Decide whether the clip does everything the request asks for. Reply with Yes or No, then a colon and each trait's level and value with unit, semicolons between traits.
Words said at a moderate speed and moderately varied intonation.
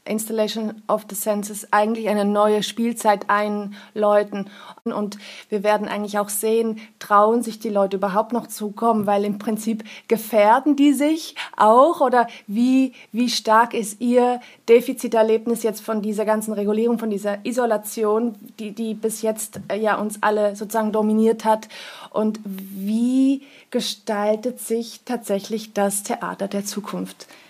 No: average, 140 wpm; narrow, 1.9 semitones